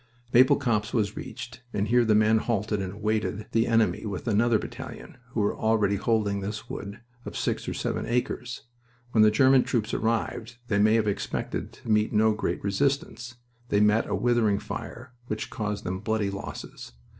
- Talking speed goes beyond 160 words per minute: Yes, average, 180 wpm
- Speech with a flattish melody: Yes, narrow, 2.2 semitones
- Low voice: Yes, low, 110 Hz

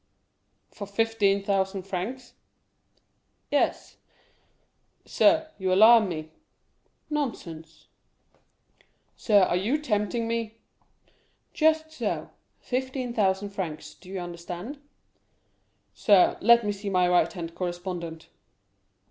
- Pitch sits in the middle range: No, high, 200 Hz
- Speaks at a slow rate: Yes, slow, 95 wpm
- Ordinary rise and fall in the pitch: Yes, average, 4.6 semitones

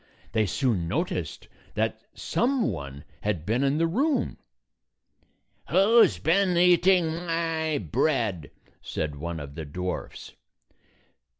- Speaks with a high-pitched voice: No, medium, 145 Hz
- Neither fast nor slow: No, slow, 115 wpm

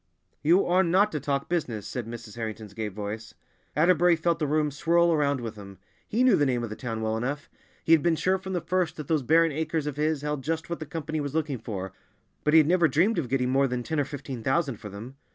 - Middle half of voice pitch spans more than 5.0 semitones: Yes, wide, 5.5 semitones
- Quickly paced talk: Yes, fast, 250 wpm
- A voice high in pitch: No, medium, 145 Hz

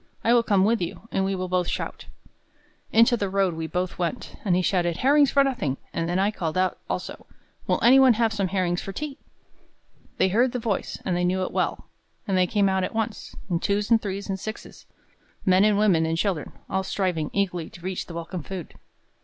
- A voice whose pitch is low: No, high, 190 Hz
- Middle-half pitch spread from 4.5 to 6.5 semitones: No, average, 3.3 semitones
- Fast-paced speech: Yes, fast, 220 wpm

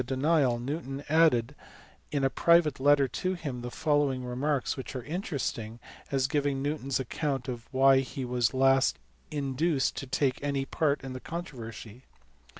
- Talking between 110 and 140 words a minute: No, average, 165 wpm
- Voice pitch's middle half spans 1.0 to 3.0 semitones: Yes, narrow, 2.4 semitones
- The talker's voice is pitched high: No, low, 135 Hz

